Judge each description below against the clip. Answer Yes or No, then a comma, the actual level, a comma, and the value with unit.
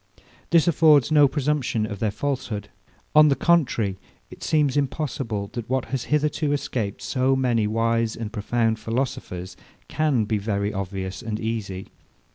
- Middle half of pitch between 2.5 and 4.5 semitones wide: No, average, 5.2 semitones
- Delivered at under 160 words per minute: Yes, average, 145 wpm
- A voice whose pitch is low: Yes, low, 115 Hz